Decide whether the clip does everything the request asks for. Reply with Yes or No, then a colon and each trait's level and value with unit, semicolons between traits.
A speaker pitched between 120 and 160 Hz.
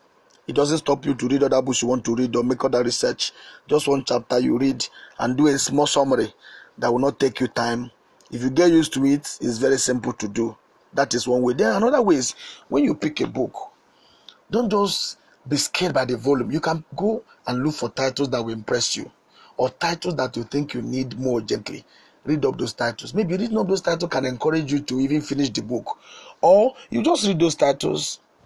Yes: medium, 140 Hz